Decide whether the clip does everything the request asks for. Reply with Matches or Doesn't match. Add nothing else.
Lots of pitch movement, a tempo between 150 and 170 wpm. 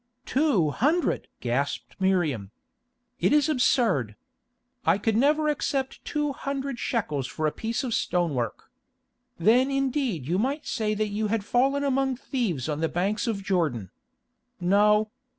Doesn't match